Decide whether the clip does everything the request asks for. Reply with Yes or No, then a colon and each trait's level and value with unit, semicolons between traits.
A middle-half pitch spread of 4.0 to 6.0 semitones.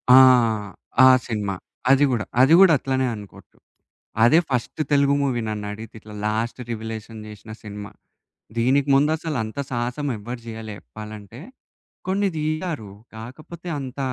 Yes: average, 4.7 semitones